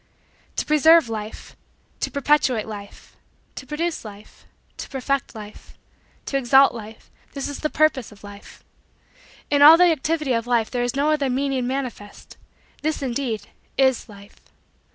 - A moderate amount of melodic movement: Yes, average, 4.6 semitones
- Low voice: No, very high, 265 Hz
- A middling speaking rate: Yes, average, 150 wpm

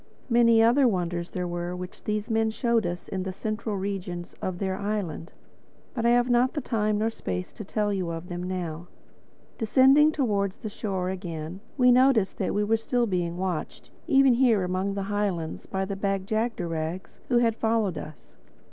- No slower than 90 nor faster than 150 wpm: No, average, 180 wpm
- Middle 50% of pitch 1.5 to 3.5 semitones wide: No, average, 4.0 semitones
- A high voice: Yes, high, 200 Hz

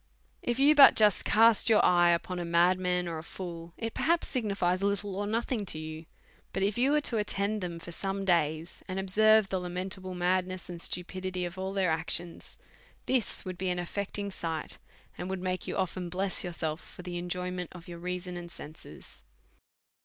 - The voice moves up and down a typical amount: No, narrow, 2.3 semitones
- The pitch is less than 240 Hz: Yes, medium, 185 Hz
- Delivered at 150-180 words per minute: No, average, 195 wpm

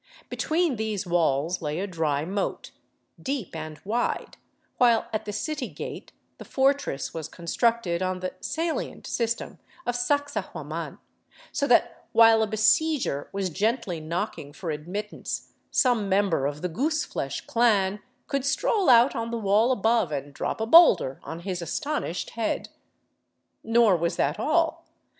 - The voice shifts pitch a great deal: Yes, wide, 6.2 semitones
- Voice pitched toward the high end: Yes, high, 210 Hz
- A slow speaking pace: No, average, 150 wpm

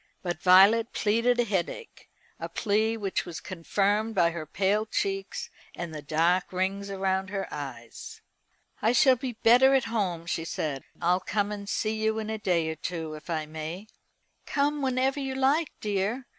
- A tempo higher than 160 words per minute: Yes, average, 170 wpm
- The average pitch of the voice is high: Yes, high, 200 Hz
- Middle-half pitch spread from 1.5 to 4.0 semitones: No, average, 5.1 semitones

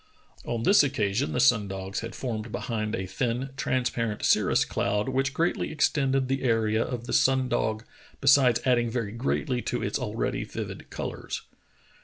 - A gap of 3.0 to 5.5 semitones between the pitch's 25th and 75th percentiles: Yes, average, 3.5 semitones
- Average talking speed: Yes, average, 160 wpm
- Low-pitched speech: Yes, low, 120 Hz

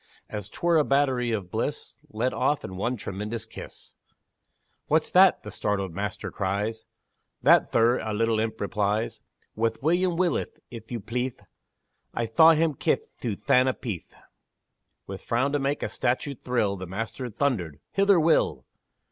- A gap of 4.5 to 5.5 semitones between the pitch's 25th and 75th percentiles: Yes, average, 4.9 semitones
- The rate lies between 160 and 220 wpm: No, average, 150 wpm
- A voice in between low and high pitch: No, low, 115 Hz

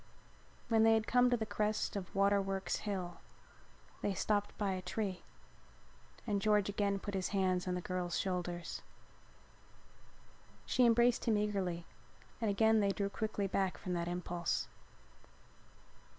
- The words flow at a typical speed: Yes, average, 145 wpm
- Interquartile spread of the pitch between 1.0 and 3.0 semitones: Yes, narrow, 2.6 semitones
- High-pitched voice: Yes, high, 200 Hz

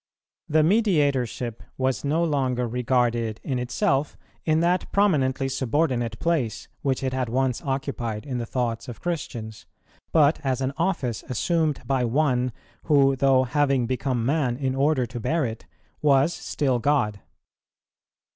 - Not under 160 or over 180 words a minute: No, average, 140 wpm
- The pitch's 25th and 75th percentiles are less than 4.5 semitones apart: Yes, average, 3.2 semitones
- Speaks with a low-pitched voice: Yes, low, 130 Hz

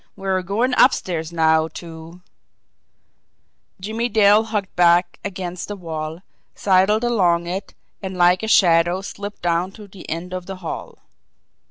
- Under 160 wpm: Yes, average, 150 wpm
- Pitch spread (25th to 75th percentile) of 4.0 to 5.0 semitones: No, average, 3.0 semitones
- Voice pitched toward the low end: No, medium, 185 Hz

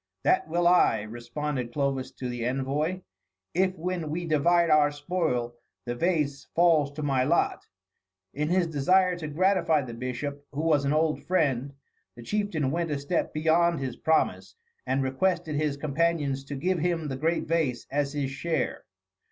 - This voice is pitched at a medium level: Yes, medium, 150 Hz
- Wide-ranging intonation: No, average, 3.7 semitones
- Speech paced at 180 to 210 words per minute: No, average, 165 wpm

